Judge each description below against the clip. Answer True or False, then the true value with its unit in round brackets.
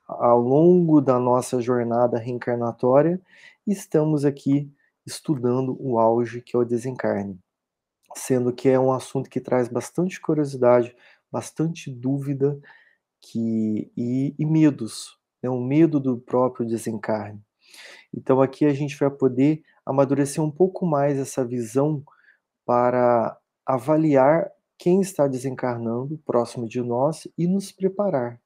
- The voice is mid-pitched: False (130 Hz)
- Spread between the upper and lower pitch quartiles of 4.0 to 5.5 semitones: False (3.4 semitones)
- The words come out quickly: False (125 wpm)